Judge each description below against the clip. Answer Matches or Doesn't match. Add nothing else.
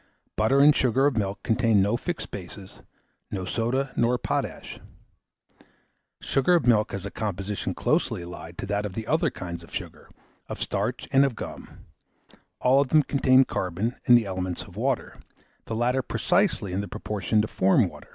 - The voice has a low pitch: Matches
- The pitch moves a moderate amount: Matches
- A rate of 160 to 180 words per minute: Matches